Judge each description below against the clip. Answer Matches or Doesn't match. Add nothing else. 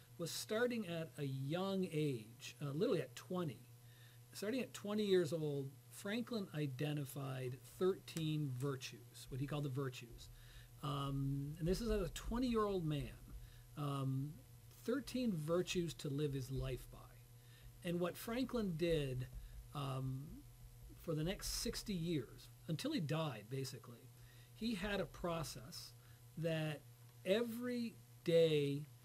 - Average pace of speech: Doesn't match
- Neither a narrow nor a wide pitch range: Doesn't match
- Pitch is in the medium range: Matches